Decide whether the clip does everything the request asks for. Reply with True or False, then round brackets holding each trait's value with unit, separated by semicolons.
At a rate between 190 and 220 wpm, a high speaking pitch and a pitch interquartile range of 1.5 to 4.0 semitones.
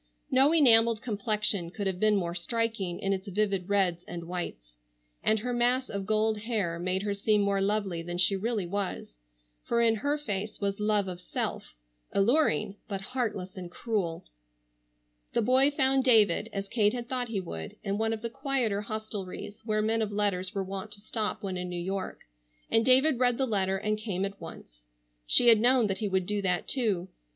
True (195 wpm; 205 Hz; 3.2 semitones)